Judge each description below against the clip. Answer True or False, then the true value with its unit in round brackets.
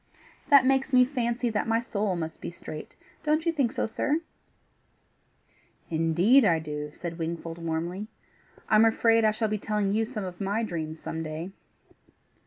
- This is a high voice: True (210 Hz)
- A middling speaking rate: True (160 wpm)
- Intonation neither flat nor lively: False (6.0 semitones)